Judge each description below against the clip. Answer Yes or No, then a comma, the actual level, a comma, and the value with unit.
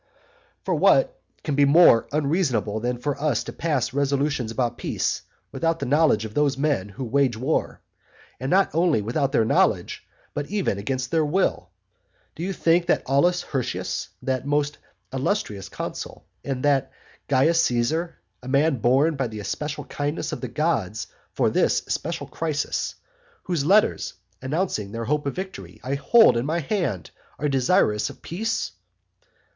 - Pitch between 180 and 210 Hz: No, medium, 140 Hz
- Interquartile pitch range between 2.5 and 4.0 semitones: No, average, 4.7 semitones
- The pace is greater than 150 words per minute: Yes, average, 160 wpm